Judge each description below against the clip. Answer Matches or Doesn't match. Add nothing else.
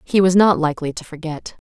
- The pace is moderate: Doesn't match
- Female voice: Matches